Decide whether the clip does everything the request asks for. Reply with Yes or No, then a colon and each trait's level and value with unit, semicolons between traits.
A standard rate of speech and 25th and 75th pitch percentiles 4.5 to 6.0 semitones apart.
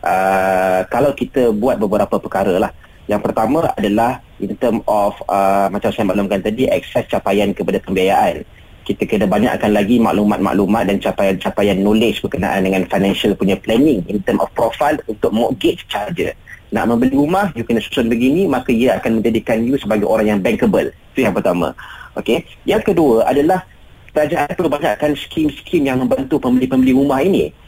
No: fast, 160 wpm; average, 5.2 semitones